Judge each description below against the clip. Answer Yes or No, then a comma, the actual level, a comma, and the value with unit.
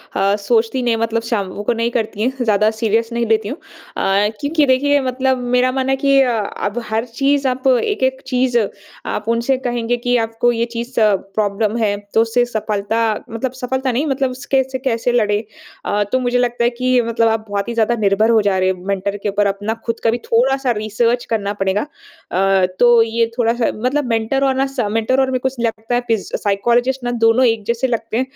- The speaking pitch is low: No, high, 235 Hz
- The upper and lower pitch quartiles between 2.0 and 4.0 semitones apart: Yes, average, 2.8 semitones